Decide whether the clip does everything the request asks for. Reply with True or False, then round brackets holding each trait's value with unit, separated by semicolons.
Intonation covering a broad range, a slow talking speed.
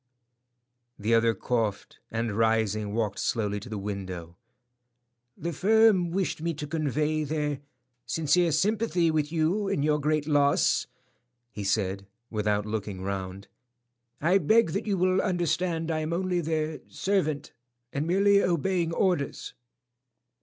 True (8.0 semitones; 130 wpm)